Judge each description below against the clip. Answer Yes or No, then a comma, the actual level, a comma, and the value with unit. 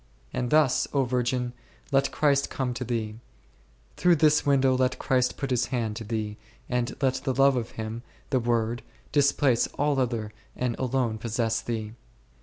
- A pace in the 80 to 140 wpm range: No, average, 165 wpm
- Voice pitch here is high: No, low, 125 Hz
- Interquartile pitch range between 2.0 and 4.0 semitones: Yes, average, 2.7 semitones